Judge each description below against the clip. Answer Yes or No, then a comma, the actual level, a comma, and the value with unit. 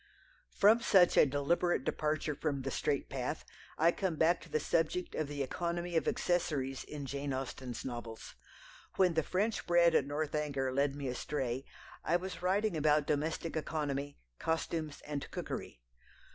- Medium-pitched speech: Yes, medium, 150 Hz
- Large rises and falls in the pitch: No, average, 3.6 semitones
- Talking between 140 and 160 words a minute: Yes, average, 155 wpm